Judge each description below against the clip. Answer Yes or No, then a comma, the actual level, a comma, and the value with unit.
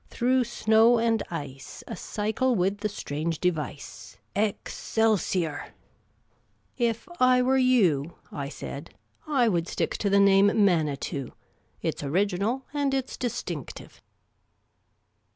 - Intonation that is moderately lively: No, wide, 6.3 semitones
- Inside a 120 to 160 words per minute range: Yes, average, 140 wpm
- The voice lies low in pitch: No, high, 205 Hz